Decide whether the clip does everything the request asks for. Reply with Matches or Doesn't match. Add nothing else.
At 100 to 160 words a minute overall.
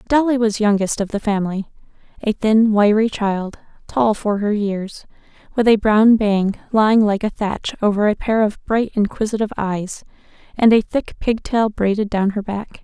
Doesn't match